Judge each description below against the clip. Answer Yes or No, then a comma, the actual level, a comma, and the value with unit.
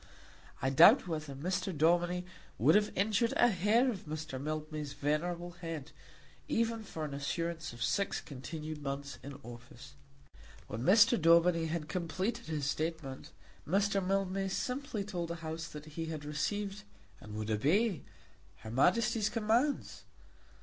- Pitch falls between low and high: Yes, medium, 165 Hz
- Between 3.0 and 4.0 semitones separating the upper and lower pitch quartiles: No, average, 5.0 semitones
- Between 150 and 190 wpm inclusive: No, average, 140 wpm